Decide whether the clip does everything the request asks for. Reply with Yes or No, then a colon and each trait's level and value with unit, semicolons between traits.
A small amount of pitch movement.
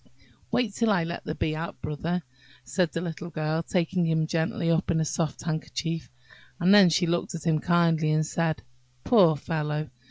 Yes: narrow, 1.8 semitones